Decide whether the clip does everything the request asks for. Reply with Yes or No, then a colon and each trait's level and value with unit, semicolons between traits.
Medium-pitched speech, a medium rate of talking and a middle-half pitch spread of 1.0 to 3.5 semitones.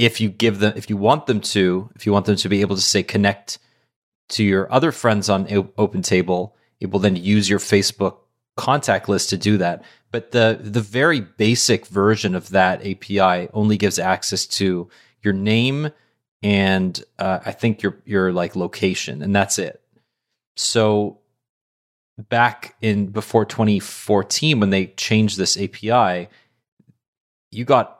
No: low, 105 Hz; average, 160 wpm; average, 2.9 semitones